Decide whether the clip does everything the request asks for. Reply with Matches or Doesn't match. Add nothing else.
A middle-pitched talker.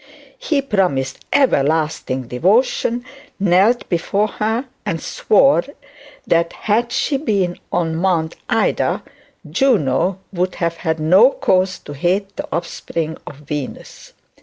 Matches